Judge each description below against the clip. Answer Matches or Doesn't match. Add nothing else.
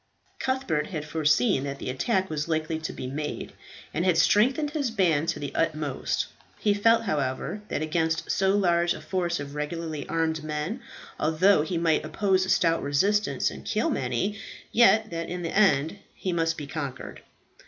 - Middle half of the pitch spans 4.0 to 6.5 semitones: Matches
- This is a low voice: Doesn't match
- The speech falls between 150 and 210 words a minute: Matches